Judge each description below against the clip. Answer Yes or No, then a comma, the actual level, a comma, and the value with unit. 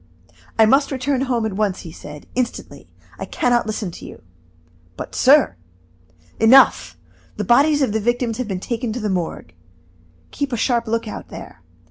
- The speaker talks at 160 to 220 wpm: Yes, average, 175 wpm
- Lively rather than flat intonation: No, average, 4.2 semitones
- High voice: Yes, high, 230 Hz